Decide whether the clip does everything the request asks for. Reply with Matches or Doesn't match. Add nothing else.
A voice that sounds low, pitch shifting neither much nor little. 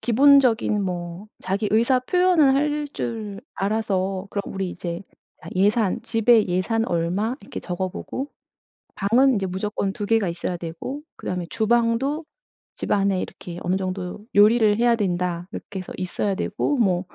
Doesn't match